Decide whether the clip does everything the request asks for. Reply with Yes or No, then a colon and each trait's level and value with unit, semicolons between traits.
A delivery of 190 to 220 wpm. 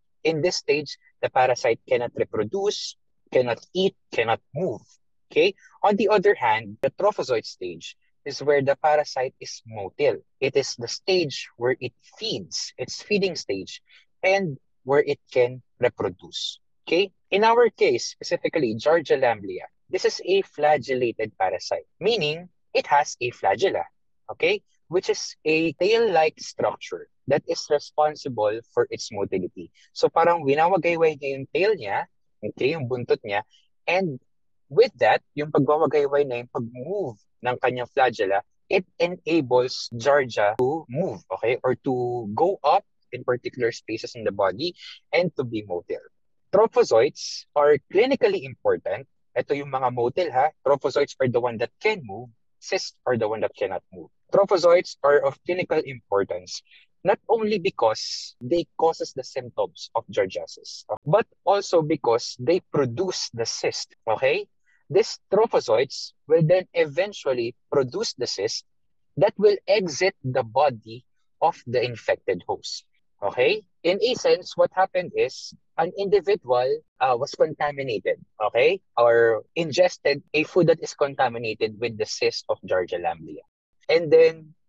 No: average, 145 wpm